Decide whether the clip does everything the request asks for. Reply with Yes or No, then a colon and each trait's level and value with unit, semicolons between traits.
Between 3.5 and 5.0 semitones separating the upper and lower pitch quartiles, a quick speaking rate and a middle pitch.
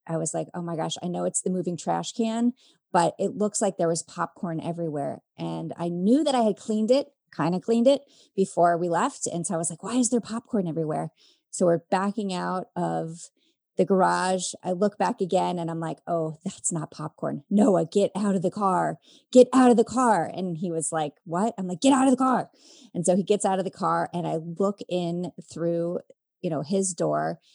Yes: average, 4.3 semitones; fast, 225 wpm; medium, 180 Hz